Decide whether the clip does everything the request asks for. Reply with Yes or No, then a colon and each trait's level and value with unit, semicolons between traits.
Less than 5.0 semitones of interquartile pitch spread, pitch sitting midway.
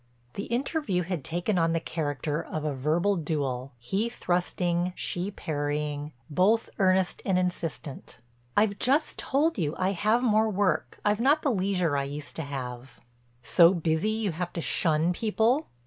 No: average, 5.3 semitones; medium, 175 Hz